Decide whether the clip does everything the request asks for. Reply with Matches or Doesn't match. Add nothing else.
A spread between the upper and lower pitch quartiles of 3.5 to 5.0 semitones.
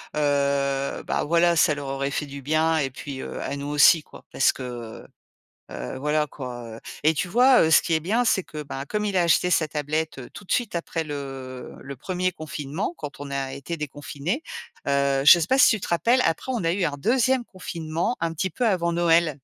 Matches